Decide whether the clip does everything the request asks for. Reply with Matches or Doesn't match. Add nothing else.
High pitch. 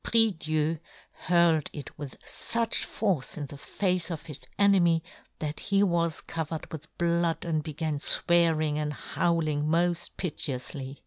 Doesn't match